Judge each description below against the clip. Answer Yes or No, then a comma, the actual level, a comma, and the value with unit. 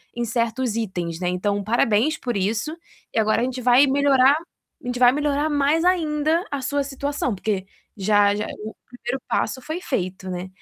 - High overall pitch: Yes, high, 245 Hz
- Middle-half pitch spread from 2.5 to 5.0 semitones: No, wide, 5.4 semitones